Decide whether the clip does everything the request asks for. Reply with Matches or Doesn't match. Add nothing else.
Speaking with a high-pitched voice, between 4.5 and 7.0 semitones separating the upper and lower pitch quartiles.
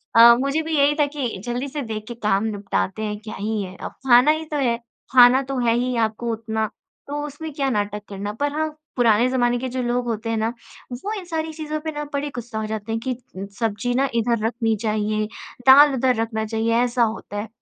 Doesn't match